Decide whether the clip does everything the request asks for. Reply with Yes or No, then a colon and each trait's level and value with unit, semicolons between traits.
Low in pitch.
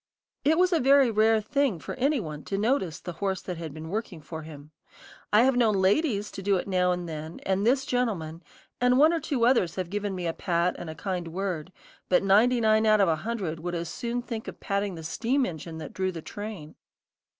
No: high, 195 Hz